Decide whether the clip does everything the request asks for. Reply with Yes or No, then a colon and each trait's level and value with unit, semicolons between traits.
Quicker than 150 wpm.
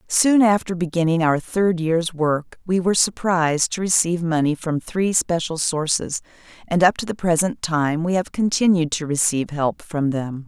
Yes: average, 180 wpm